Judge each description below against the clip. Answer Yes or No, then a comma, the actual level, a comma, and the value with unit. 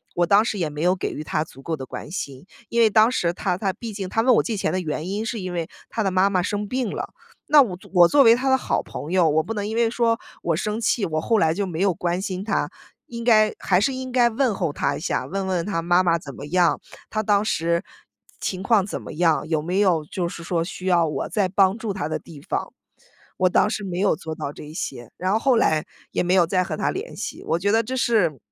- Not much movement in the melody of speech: No, average, 4.4 semitones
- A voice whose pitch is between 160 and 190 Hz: Yes, medium, 185 Hz